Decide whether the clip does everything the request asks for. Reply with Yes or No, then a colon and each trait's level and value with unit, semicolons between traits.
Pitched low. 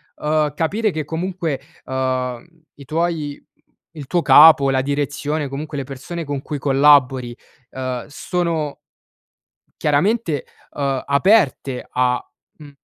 No: medium, 145 Hz